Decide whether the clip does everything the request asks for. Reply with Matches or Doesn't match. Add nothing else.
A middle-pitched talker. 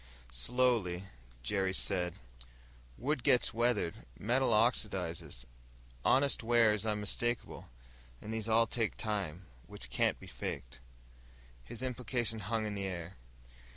Doesn't match